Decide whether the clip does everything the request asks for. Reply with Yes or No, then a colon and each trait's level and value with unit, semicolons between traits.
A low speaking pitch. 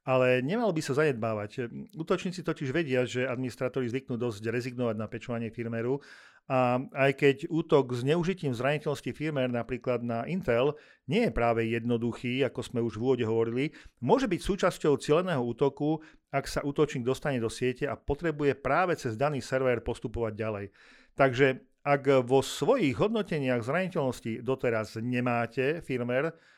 Yes: low, 130 Hz